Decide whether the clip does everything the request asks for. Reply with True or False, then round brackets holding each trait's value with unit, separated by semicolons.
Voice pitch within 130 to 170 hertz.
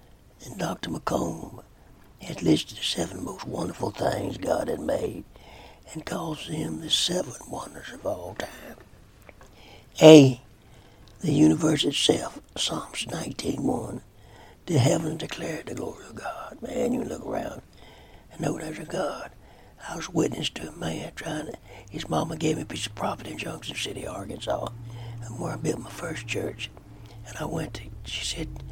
False (115 Hz)